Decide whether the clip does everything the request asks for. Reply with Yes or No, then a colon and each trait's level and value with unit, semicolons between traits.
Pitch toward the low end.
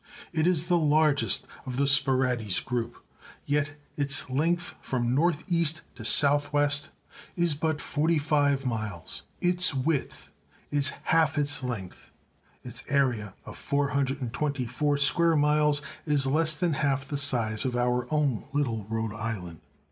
No: medium, 145 Hz